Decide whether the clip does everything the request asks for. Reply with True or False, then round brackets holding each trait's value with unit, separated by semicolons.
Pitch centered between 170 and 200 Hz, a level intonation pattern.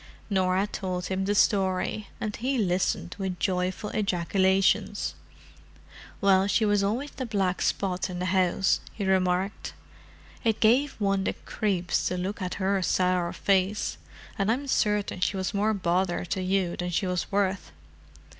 True (190 Hz; 2.0 semitones)